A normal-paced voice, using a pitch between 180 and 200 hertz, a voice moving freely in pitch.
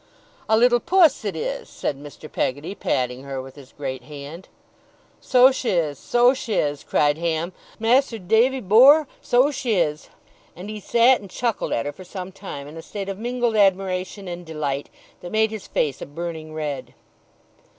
Yes: average, 180 wpm; medium, 185 Hz; wide, 7.8 semitones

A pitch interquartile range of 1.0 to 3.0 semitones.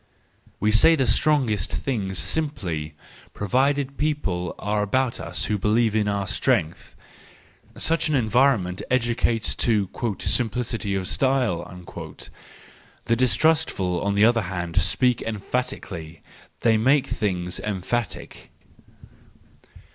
No: average, 5.0 semitones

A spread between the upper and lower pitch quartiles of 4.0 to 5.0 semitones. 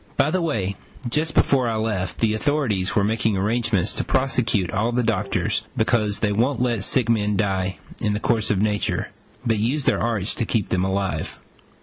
No: average, 3.0 semitones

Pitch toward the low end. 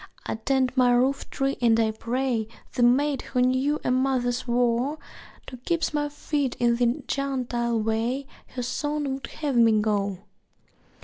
No: very high, 250 Hz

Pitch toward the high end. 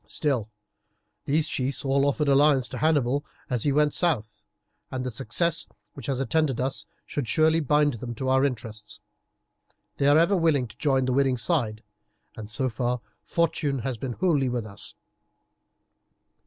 No: low, 135 Hz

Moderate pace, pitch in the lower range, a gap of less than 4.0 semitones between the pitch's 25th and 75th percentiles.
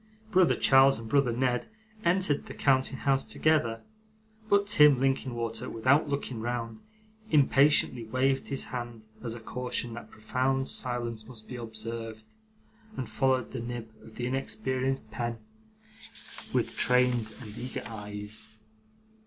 No: slow, 130 wpm; low, 125 Hz; average, 2.8 semitones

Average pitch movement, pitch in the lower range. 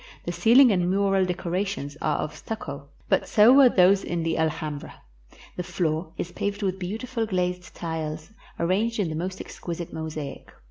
No: average, 3.9 semitones; medium, 180 Hz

